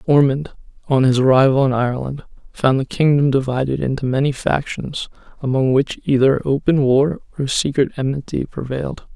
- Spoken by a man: Yes, male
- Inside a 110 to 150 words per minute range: Yes, average, 145 wpm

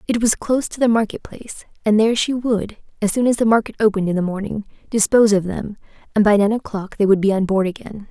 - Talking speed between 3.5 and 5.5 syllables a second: No, 6.5 syllables/s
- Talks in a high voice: Yes, high, 210 Hz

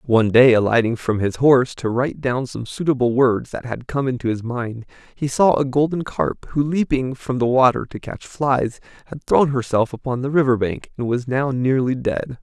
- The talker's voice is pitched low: Yes, low, 125 Hz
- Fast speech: Yes, fast, 210 wpm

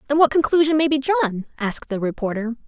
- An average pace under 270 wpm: Yes, average, 200 wpm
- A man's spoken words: No, female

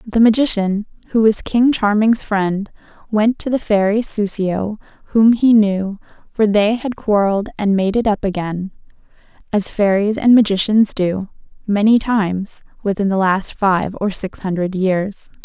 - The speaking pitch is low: No, high, 205 Hz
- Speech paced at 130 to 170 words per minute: Yes, average, 150 wpm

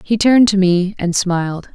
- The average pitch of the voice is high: Yes, high, 195 Hz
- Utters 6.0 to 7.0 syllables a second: No, 4.9 syllables/s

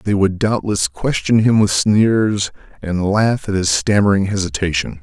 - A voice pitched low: Yes, low, 100 Hz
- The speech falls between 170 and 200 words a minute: No, average, 155 wpm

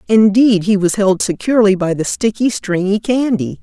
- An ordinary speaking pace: Yes, average, 165 wpm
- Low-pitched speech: No, high, 205 Hz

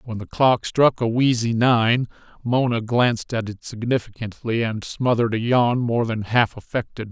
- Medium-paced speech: Yes, average, 170 wpm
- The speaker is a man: Yes, male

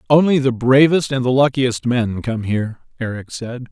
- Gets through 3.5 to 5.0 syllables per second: Yes, 4.9 syllables/s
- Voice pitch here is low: Yes, low, 125 Hz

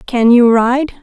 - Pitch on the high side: Yes, high, 245 Hz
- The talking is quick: No, average, 175 wpm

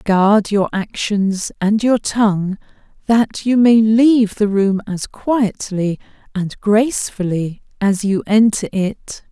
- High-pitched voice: Yes, high, 210 Hz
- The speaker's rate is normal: No, slow, 130 wpm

